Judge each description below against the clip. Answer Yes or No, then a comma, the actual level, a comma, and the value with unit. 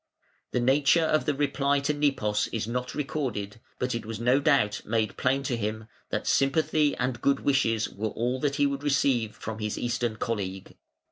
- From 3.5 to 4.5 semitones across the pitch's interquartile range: Yes, average, 4.1 semitones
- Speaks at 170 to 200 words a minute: Yes, average, 185 wpm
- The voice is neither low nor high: No, low, 125 Hz